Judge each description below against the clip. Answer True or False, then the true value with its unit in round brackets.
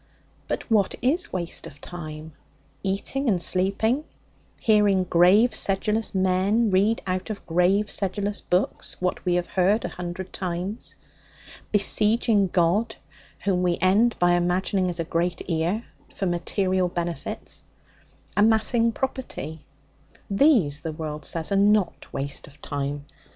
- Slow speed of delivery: True (130 wpm)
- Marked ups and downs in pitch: False (3.3 semitones)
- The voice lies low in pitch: False (185 Hz)